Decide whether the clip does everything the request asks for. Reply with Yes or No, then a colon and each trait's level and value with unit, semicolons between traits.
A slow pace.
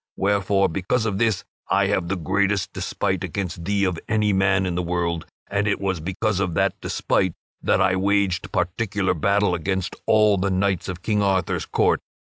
No: average, 180 wpm